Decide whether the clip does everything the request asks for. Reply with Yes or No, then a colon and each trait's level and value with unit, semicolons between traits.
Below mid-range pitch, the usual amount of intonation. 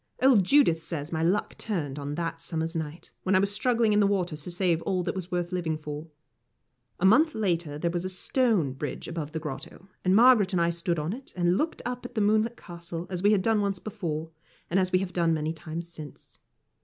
No: medium, 175 Hz; average, 3.8 semitones